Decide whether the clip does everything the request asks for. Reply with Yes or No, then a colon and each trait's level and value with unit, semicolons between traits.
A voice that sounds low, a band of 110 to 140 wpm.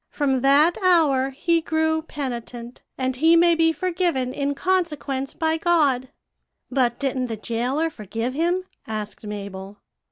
No: very high, 275 Hz; slow, 135 wpm